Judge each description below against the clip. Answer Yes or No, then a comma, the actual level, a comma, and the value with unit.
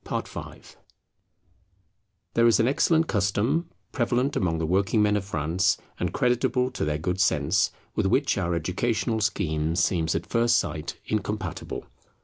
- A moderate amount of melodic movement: No, wide, 5.8 semitones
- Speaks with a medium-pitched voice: No, low, 100 Hz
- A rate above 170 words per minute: No, average, 150 wpm